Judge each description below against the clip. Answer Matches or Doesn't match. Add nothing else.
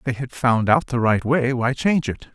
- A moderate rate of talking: Doesn't match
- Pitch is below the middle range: Matches